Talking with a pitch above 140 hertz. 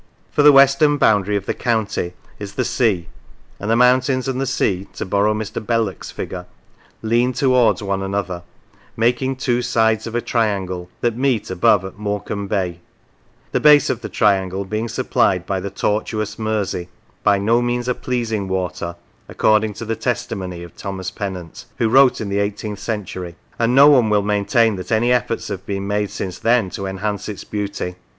No: low, 105 Hz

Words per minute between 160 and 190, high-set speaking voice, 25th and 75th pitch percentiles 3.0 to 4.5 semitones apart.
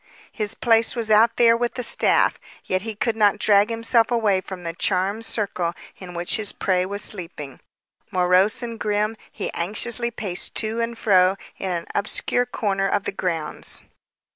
Yes: average, 170 wpm; high, 205 Hz; average, 3.5 semitones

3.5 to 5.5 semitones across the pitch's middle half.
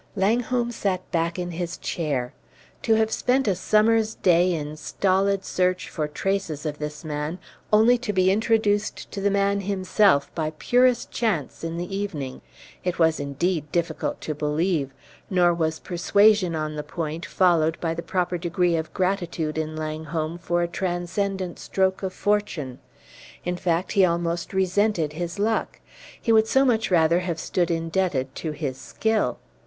Yes: average, 3.8 semitones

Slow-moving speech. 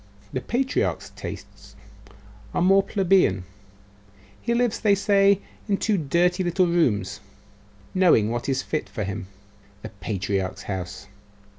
Yes: slow, 125 wpm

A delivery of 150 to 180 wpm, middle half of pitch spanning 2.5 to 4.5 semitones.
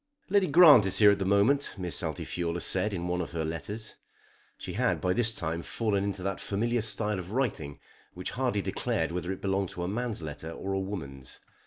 No: fast, 205 wpm; average, 3.8 semitones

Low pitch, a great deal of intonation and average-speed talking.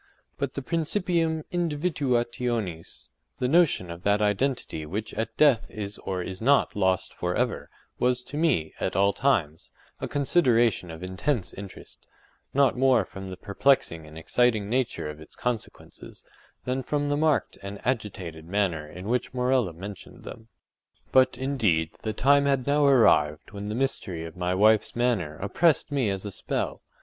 Yes: low, 110 Hz; wide, 6.5 semitones; average, 155 wpm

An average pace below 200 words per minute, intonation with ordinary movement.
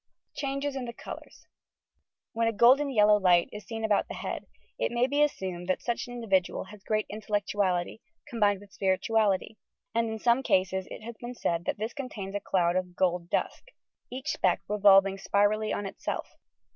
Yes: average, 180 wpm; average, 3.6 semitones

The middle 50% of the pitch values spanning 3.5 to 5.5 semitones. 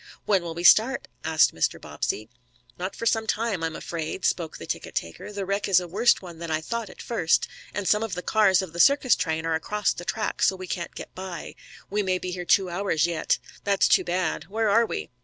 Yes: average, 3.8 semitones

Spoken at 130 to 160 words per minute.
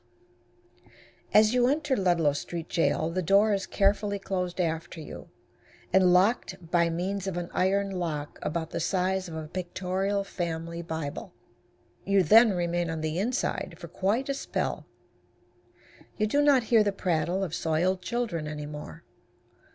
Yes: average, 150 wpm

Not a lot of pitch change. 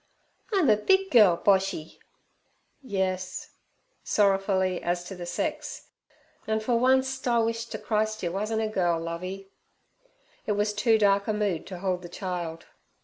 No: average, 3.4 semitones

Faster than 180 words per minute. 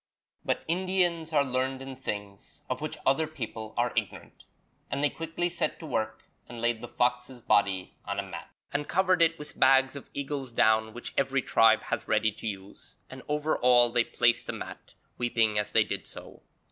Yes: average, 190 wpm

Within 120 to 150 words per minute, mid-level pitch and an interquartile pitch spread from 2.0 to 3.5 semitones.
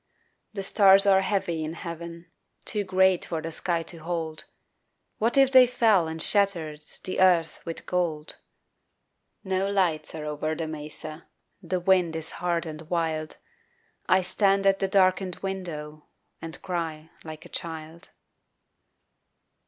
Yes: average, 140 wpm; medium, 170 Hz; average, 3.2 semitones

